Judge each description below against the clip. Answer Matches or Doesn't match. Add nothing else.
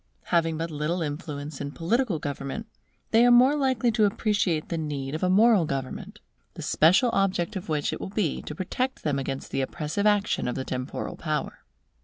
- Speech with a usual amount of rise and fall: Doesn't match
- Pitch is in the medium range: Matches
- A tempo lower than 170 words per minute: Doesn't match